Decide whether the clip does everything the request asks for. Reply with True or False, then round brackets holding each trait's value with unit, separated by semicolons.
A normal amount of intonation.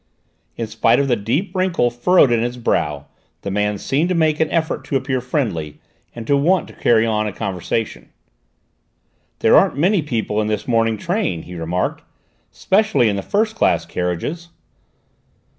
False (7.4 semitones)